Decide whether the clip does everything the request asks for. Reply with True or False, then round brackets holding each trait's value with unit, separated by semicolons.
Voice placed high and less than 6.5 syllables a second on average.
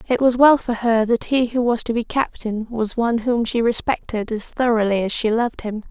True (230 Hz; 5.3 syllables/s)